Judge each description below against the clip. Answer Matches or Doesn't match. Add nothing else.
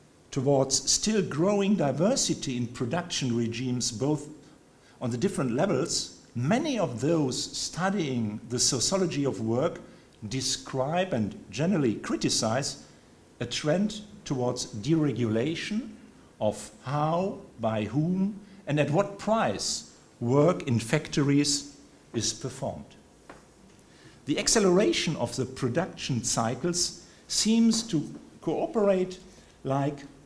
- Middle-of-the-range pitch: Matches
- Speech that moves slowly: Matches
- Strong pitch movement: Matches